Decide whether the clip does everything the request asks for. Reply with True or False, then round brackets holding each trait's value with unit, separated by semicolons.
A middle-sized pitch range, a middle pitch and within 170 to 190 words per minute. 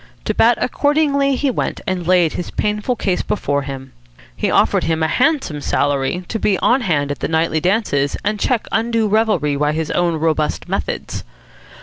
False (7.0 semitones; 180 Hz; 180 wpm)